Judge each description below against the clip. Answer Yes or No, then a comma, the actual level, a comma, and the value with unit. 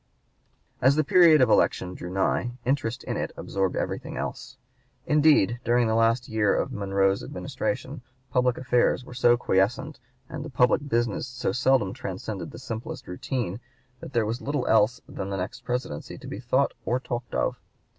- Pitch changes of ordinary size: Yes, average, 4.0 semitones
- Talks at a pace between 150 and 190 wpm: Yes, average, 170 wpm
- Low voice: Yes, low, 120 Hz